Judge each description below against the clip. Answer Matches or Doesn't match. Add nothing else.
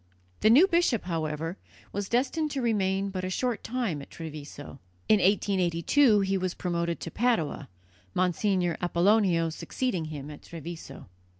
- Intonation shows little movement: Doesn't match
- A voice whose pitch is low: Doesn't match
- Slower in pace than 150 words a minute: Matches